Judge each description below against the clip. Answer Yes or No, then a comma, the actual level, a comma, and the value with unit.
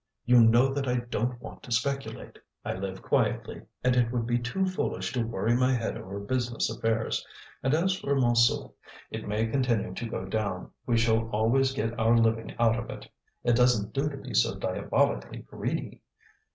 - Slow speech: No, average, 185 wpm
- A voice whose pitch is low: Yes, low, 120 Hz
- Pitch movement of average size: No, narrow, 2.1 semitones